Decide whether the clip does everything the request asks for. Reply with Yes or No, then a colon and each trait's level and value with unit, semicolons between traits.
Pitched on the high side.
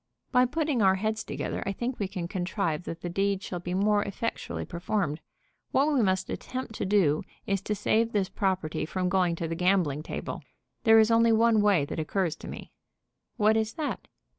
Yes: high, 195 Hz